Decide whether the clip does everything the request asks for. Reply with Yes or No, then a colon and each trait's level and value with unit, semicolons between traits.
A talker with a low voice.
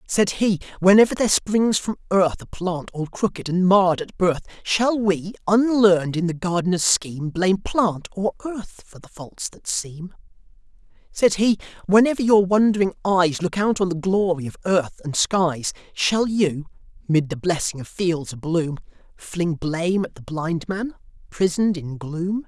No: medium, 185 Hz